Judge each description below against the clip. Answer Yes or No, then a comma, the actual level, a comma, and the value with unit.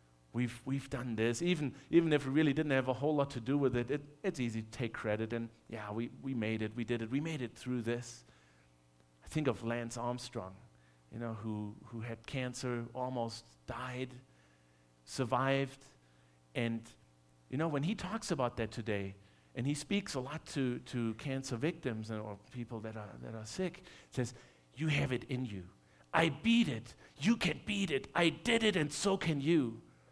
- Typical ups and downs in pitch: Yes, average, 4.5 semitones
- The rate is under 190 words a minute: No, average, 195 wpm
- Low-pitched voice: Yes, low, 120 Hz